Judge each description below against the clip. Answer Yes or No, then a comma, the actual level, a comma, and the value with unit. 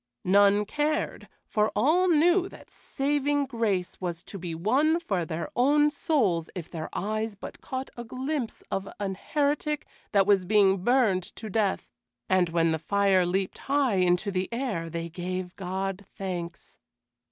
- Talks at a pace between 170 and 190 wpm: No, average, 155 wpm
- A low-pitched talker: No, high, 200 Hz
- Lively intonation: Yes, wide, 6.6 semitones